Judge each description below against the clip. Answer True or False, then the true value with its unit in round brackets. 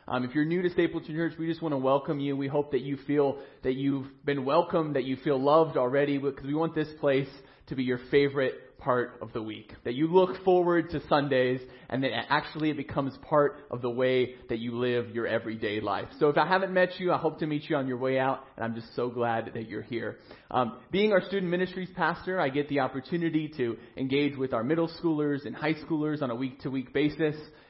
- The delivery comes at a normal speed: False (235 wpm)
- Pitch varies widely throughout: False (3.7 semitones)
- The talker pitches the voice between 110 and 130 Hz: False (140 Hz)